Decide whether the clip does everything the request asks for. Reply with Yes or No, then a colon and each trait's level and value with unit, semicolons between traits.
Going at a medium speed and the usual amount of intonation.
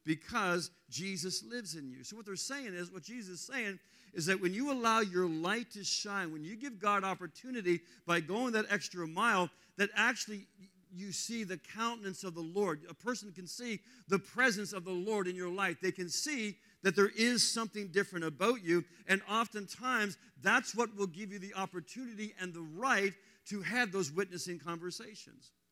Yes: average, 190 wpm; average, 3.9 semitones